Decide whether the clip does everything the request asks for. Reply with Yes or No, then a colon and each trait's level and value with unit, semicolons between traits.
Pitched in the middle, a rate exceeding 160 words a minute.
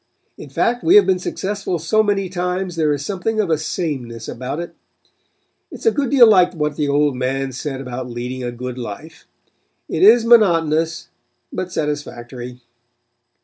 Yes: medium, 160 Hz; average, 170 wpm